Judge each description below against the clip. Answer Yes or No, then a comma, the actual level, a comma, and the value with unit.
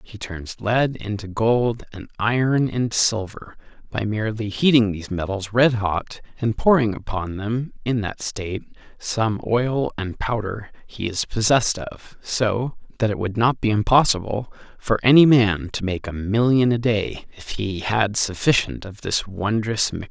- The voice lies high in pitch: No, low, 110 Hz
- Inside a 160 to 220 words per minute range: Yes, average, 165 wpm